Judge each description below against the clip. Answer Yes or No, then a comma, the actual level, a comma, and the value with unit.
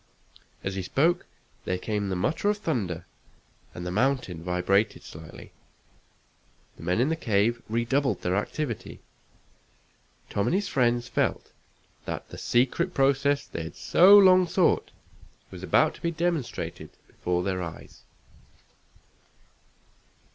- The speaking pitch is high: No, low, 120 Hz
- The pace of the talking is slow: Yes, slow, 130 wpm